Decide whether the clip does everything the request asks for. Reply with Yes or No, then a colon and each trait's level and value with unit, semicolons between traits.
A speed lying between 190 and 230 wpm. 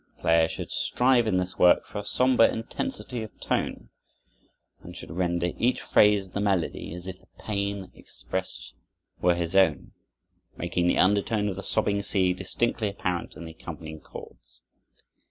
No: average, 165 wpm